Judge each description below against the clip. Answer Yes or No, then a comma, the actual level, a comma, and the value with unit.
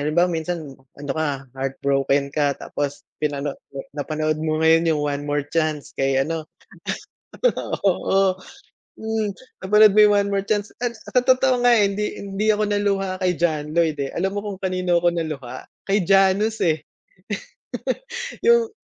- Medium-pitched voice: Yes, medium, 170 Hz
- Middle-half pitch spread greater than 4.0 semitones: Yes, average, 5.3 semitones